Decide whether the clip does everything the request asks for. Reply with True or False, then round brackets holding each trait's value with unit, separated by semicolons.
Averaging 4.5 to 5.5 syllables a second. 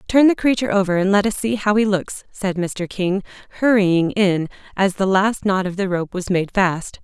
True (4.9 syllables/s)